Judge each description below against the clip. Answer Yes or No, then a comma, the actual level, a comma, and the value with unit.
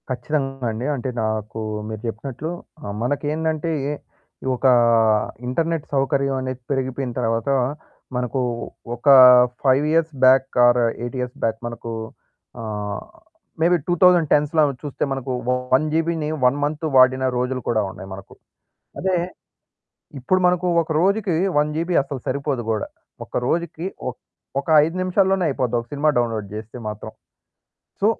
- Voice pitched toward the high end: No, low, 135 Hz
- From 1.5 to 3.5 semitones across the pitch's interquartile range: No, average, 4.7 semitones